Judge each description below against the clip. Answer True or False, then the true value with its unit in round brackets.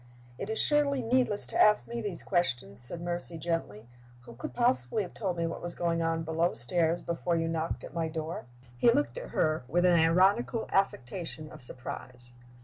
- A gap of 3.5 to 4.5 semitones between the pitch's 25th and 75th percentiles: True (3.9 semitones)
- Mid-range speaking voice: True (170 Hz)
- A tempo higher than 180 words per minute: True (190 wpm)